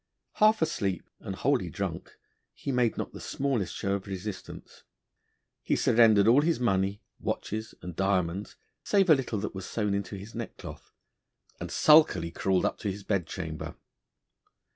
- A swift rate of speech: No, average, 155 wpm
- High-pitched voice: No, low, 100 Hz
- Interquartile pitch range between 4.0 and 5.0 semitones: Yes, average, 4.5 semitones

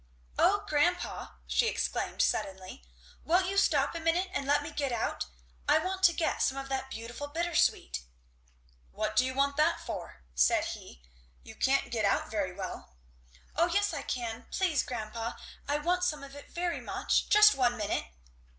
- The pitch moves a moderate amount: No, wide, 6.3 semitones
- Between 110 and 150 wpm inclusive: No, average, 175 wpm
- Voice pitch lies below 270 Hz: No, very high, 290 Hz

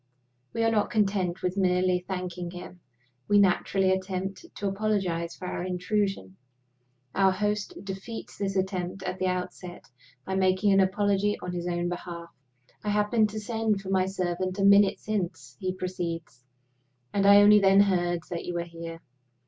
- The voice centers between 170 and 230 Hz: Yes, high, 190 Hz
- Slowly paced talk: No, average, 165 wpm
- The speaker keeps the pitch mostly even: Yes, narrow, 2.2 semitones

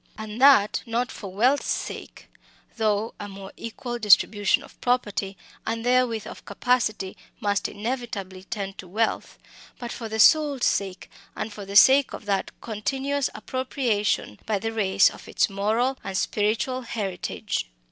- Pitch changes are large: No, average, 3.6 semitones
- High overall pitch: Yes, high, 220 Hz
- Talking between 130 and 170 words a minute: Yes, average, 145 wpm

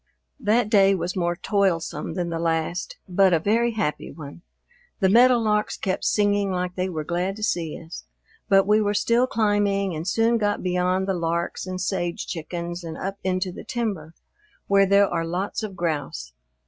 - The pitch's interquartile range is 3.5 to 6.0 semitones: No, average, 3.1 semitones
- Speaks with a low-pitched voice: No, medium, 185 Hz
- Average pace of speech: Yes, average, 175 wpm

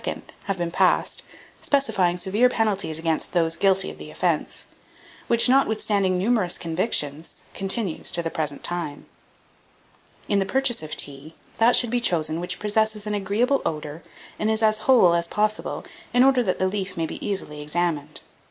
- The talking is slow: No, average, 165 wpm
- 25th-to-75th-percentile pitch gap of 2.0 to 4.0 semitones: No, average, 4.8 semitones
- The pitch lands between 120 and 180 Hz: No, high, 190 Hz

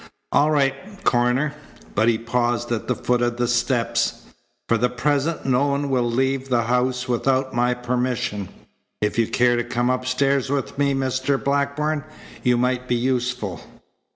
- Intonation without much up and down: Yes, narrow, 2.0 semitones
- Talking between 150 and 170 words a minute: Yes, average, 160 wpm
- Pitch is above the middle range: No, low, 125 Hz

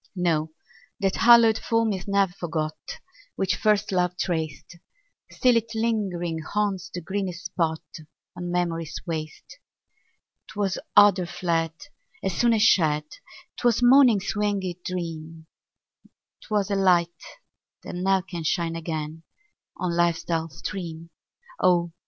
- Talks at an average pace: No, slow, 120 wpm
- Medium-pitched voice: Yes, medium, 180 Hz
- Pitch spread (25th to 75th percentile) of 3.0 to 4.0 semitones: Yes, average, 3.5 semitones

